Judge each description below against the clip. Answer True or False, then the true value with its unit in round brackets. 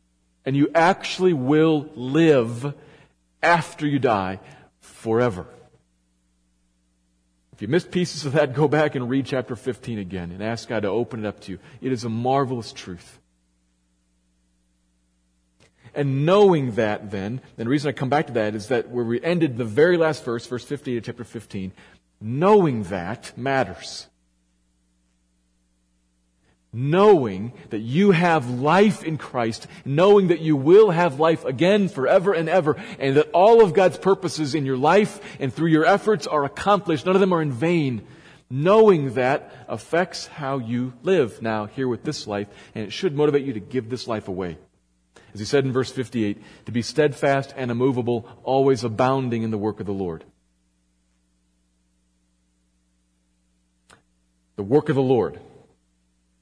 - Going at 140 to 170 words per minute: True (155 wpm)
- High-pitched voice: False (125 Hz)